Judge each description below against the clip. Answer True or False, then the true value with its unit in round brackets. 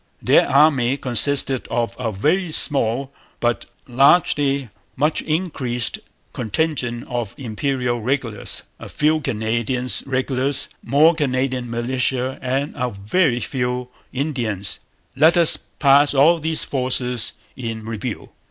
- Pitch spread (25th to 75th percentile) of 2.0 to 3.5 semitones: True (3.1 semitones)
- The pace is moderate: False (115 wpm)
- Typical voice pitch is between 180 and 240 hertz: False (130 Hz)